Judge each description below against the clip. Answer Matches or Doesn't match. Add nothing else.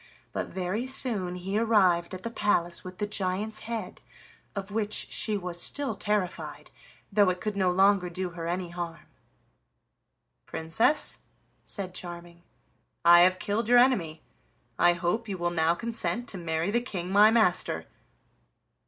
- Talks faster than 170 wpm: Doesn't match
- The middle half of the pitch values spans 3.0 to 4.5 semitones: Matches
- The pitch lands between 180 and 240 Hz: Matches